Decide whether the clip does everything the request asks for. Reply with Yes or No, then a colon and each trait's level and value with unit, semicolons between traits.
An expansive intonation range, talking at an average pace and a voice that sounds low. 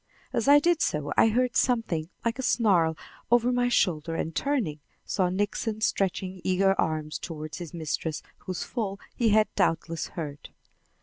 No: wide, 6.3 semitones; average, 160 wpm; high, 190 Hz